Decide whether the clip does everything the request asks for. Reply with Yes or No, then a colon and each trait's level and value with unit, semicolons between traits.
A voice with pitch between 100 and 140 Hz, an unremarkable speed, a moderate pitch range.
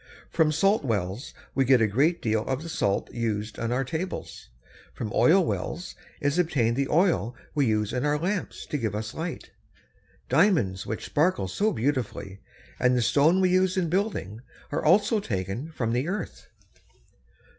No: low, 135 Hz; average, 165 wpm; wide, 7.5 semitones